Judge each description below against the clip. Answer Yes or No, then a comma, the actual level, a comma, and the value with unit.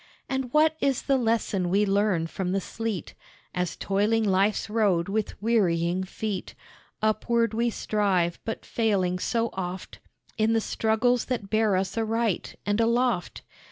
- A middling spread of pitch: Yes, average, 3.2 semitones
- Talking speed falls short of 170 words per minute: Yes, average, 145 wpm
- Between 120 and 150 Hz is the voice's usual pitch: No, high, 215 Hz